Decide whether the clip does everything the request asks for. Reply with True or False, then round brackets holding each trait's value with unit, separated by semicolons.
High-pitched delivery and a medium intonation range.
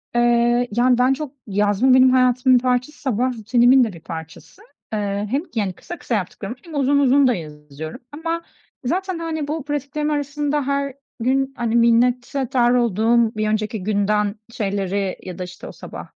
True (245 Hz; 4.7 semitones)